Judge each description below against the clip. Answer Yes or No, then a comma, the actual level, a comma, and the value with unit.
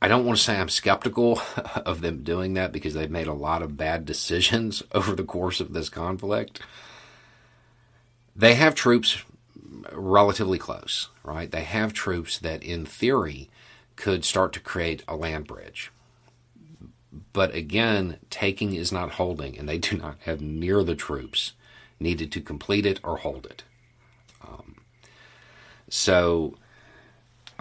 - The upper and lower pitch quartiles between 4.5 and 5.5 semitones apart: Yes, average, 5.0 semitones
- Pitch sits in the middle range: No, very low, 95 Hz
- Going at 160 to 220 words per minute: No, average, 145 wpm